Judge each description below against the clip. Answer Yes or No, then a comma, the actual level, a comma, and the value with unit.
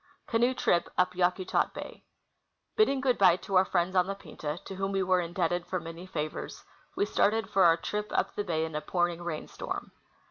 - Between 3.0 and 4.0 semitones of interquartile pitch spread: No, narrow, 2.4 semitones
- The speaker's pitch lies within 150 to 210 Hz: Yes, medium, 185 Hz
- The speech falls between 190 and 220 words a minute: Yes, fast, 205 wpm